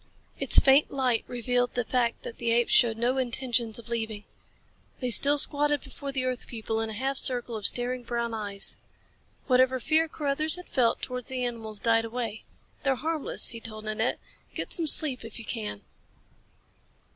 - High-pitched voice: Yes, high, 245 Hz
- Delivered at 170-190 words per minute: Yes, average, 175 wpm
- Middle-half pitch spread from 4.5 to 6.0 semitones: No, average, 2.7 semitones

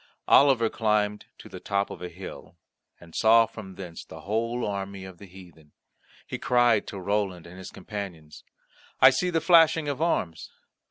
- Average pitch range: Yes, average, 4.2 semitones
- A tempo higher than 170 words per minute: No, average, 165 wpm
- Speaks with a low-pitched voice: Yes, low, 100 Hz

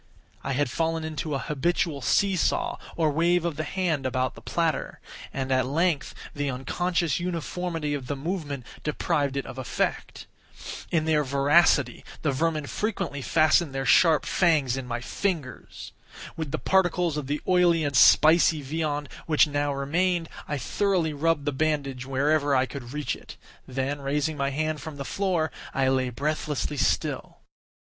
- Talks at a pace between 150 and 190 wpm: Yes, average, 160 wpm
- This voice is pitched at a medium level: Yes, medium, 150 Hz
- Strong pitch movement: No, average, 3.1 semitones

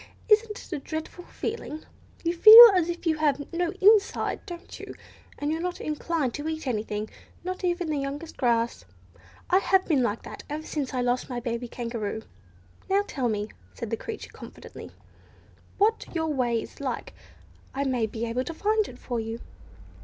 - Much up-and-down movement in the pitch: Yes, wide, 6.6 semitones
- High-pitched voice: Yes, very high, 295 Hz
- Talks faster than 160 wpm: Yes, average, 175 wpm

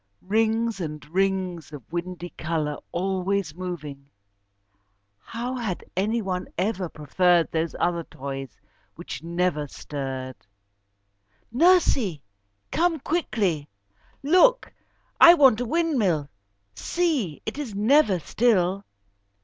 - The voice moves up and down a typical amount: No, wide, 6.5 semitones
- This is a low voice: No, medium, 185 Hz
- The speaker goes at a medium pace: No, slow, 100 wpm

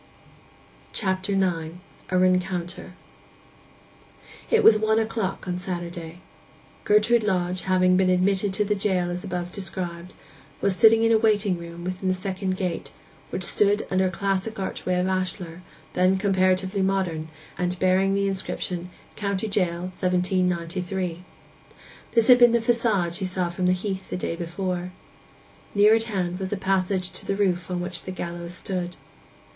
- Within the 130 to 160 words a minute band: Yes, average, 150 wpm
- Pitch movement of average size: No, narrow, 1.8 semitones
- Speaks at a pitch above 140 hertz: Yes, medium, 185 Hz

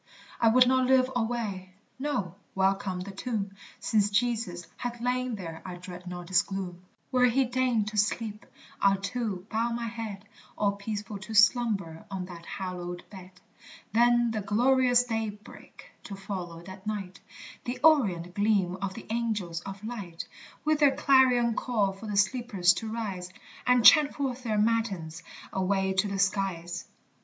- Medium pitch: No, high, 210 Hz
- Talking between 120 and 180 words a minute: Yes, average, 155 wpm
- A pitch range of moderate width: Yes, average, 4.0 semitones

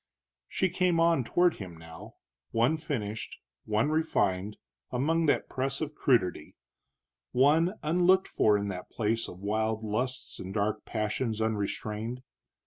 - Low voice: Yes, low, 115 Hz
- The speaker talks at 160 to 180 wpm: No, slow, 135 wpm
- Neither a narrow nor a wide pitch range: No, wide, 6.6 semitones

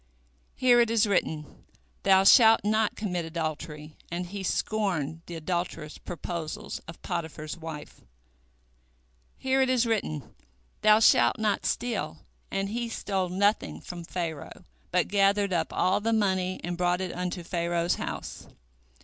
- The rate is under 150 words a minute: Yes, average, 140 wpm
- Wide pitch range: No, average, 4.0 semitones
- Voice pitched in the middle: Yes, medium, 180 Hz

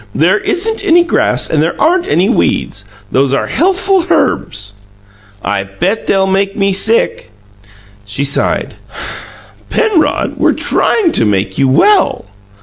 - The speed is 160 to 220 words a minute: No, slow, 135 wpm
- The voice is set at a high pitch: Yes, high, 195 Hz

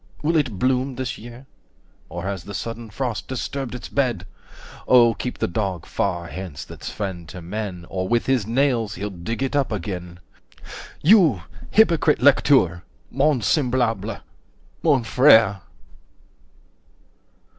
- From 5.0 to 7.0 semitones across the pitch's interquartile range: Yes, wide, 5.5 semitones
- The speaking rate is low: Yes, slow, 130 wpm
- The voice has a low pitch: Yes, low, 115 Hz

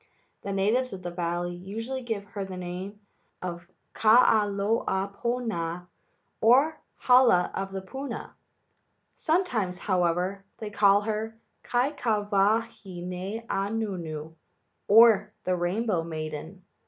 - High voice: Yes, high, 200 Hz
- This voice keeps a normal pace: No, slow, 100 wpm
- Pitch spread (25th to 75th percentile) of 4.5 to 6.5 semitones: No, average, 3.8 semitones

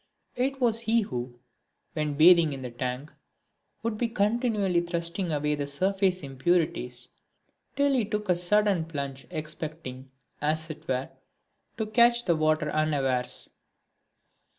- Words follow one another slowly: Yes, slow, 130 wpm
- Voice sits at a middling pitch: Yes, medium, 165 Hz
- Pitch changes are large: Yes, wide, 6.7 semitones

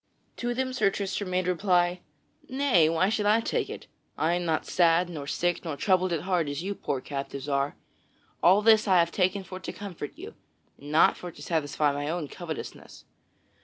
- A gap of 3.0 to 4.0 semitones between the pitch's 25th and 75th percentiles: Yes, average, 3.7 semitones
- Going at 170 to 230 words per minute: Yes, average, 195 wpm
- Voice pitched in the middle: Yes, medium, 175 Hz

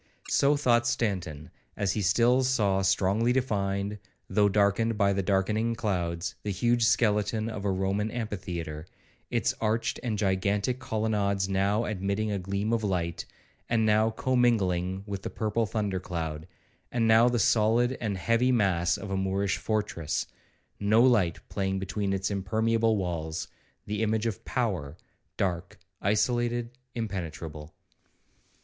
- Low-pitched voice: Yes, low, 105 Hz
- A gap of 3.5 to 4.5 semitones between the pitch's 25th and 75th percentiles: No, average, 3.0 semitones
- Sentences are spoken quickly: No, slow, 135 wpm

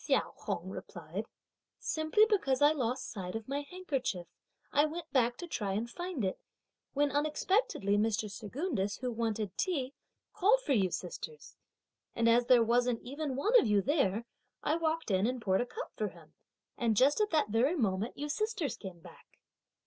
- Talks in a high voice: Yes, very high, 255 Hz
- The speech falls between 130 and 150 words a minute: No, average, 180 wpm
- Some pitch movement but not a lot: No, wide, 6.4 semitones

